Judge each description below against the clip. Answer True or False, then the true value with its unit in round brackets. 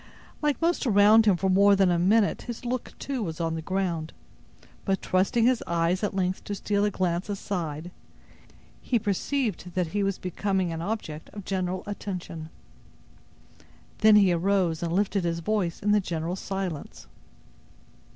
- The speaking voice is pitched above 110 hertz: True (190 Hz)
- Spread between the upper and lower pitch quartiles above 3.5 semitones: False (3.2 semitones)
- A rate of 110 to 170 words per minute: True (160 wpm)